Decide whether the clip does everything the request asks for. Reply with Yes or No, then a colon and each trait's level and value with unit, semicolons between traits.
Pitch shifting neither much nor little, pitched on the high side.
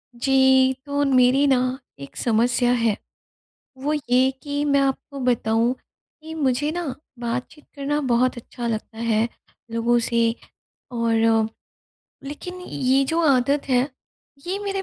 Yes: average, 3.2 semitones; very high, 255 Hz